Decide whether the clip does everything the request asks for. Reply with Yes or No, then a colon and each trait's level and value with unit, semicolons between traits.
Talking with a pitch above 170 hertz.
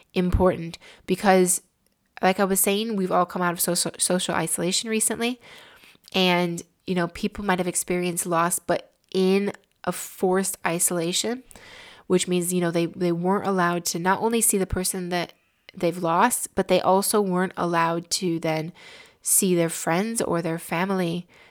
Yes: medium, 185 Hz